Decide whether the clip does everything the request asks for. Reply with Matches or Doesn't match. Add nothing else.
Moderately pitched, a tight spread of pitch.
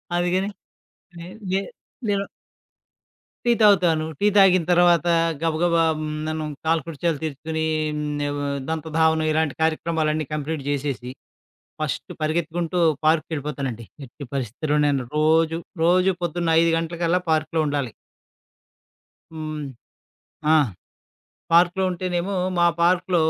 Matches